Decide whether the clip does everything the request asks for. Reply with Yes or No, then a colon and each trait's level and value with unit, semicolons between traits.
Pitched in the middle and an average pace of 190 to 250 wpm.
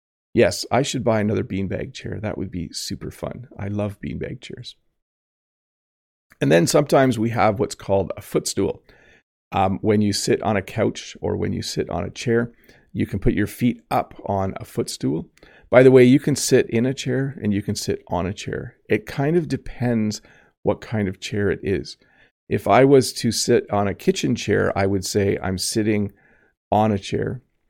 No: low, 105 Hz; average, 195 wpm